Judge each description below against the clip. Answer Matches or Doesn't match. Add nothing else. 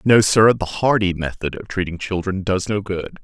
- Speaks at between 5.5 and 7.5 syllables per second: Doesn't match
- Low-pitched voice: Matches